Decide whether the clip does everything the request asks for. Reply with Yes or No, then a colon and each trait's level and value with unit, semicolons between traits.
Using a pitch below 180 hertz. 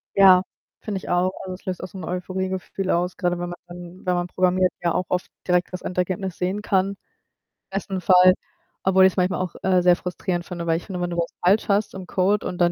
No: medium, 185 Hz